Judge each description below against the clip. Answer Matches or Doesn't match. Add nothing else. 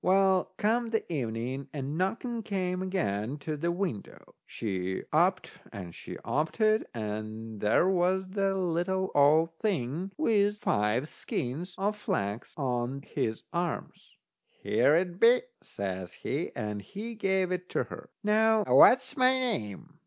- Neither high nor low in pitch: Matches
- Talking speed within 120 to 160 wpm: Matches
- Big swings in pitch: Matches